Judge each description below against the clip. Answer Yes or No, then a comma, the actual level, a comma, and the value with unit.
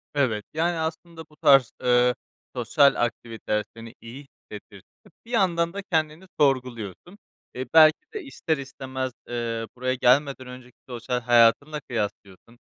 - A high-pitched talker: No, low, 130 Hz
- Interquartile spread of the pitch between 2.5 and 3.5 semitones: No, average, 4.9 semitones